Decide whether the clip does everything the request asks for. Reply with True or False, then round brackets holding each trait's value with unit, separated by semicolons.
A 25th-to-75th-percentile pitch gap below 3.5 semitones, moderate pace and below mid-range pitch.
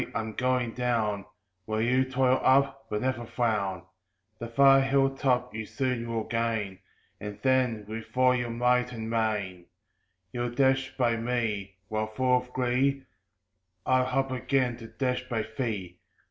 True (2.7 semitones; 150 wpm; 120 Hz)